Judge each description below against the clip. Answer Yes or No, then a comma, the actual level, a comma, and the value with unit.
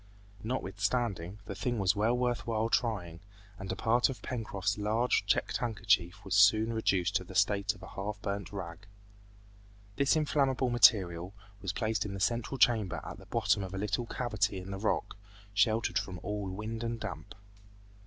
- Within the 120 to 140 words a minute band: No, average, 175 wpm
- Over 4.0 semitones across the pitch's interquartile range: No, average, 3.1 semitones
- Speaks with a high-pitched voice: No, low, 105 Hz